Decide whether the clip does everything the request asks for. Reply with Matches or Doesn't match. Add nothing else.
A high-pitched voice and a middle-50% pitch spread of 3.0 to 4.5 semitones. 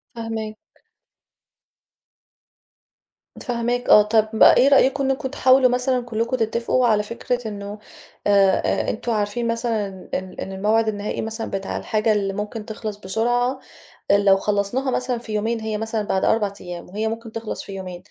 Doesn't match